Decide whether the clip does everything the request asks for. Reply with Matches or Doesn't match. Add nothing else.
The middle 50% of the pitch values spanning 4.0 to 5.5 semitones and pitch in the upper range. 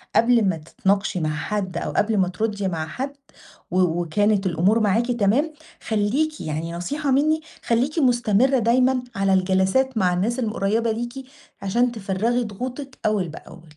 Matches